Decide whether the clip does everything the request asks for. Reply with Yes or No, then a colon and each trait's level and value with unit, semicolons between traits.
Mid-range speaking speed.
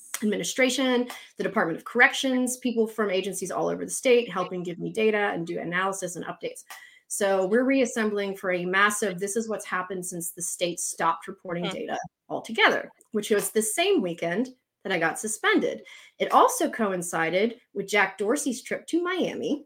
Yes: average, 170 wpm